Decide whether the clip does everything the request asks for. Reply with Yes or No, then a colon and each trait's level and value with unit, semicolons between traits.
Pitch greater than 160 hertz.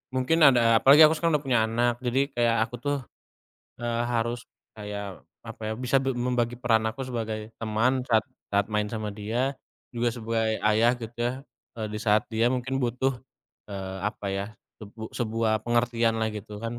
No: low, 115 Hz